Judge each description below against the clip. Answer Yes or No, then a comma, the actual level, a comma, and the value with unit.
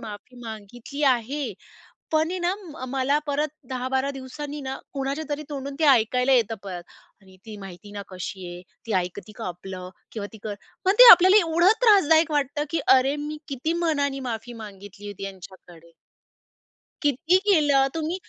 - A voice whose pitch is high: Yes, very high, 265 Hz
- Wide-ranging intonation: Yes, wide, 6.4 semitones